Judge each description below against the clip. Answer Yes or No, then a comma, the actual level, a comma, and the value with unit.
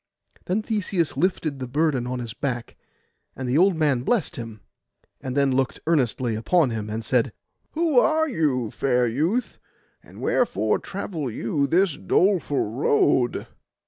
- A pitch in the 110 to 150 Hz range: Yes, medium, 140 Hz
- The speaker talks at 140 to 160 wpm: Yes, average, 145 wpm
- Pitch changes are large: Yes, wide, 6.4 semitones